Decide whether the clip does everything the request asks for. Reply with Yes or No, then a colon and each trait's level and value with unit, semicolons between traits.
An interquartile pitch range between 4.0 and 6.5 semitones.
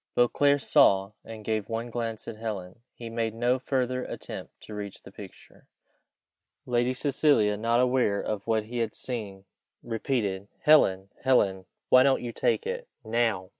No: average, 3.4 semitones